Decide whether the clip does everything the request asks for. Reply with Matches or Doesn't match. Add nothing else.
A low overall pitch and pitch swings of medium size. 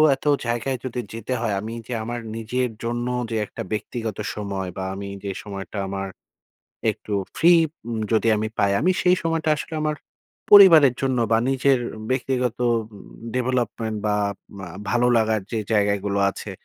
Matches